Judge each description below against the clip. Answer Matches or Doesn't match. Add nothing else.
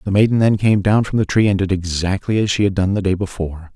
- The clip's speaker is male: Matches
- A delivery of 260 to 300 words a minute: Matches